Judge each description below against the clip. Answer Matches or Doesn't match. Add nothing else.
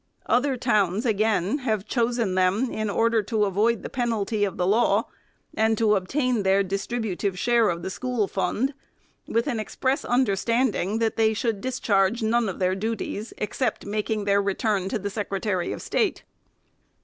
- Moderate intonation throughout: Matches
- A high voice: Matches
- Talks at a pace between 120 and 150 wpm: Doesn't match